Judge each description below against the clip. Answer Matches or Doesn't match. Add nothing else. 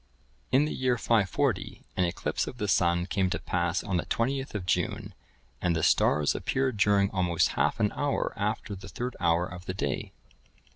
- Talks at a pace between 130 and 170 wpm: Doesn't match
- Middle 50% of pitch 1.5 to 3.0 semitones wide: Doesn't match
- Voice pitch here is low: Matches